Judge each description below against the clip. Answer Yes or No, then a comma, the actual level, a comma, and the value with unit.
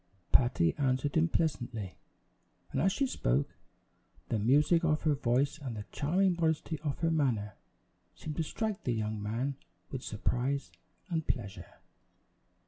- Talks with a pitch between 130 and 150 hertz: Yes, medium, 140 Hz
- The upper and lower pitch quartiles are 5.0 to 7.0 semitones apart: Yes, wide, 5.5 semitones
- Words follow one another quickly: No, average, 140 wpm